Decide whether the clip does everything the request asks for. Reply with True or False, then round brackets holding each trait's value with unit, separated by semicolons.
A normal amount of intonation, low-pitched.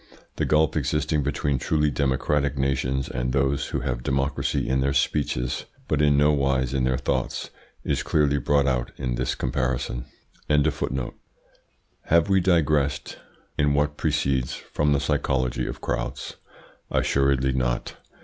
False (2.1 semitones; 70 Hz)